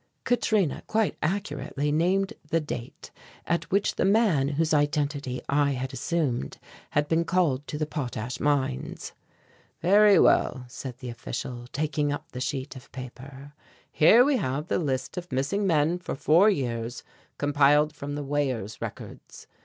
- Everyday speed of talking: Yes, average, 150 wpm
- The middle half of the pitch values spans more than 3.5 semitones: Yes, average, 4.1 semitones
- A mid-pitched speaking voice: Yes, medium, 145 Hz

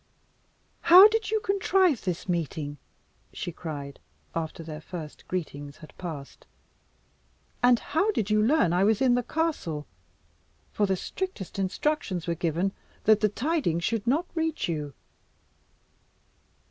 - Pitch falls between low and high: No, high, 195 Hz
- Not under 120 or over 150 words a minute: Yes, slow, 135 wpm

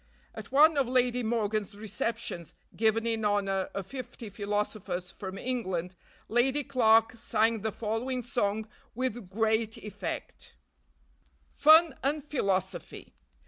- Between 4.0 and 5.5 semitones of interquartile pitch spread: No, average, 3.5 semitones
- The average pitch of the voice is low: No, high, 220 Hz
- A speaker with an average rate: No, slow, 115 wpm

